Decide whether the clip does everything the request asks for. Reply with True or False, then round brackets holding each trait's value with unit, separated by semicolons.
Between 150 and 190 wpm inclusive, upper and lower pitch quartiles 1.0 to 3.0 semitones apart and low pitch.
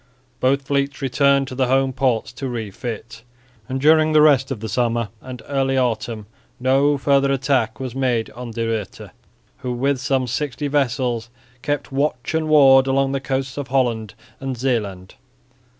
True (165 wpm; 2.4 semitones; 130 Hz)